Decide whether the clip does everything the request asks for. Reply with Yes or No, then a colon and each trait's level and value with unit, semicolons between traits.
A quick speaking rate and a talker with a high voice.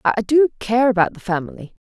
No: average, 190 wpm; high, 225 Hz